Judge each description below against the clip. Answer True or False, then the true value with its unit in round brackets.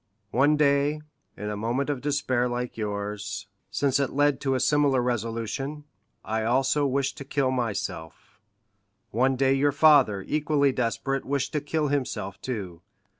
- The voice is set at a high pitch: False (130 Hz)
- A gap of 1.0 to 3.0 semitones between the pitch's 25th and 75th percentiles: False (4.0 semitones)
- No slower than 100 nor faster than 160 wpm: True (150 wpm)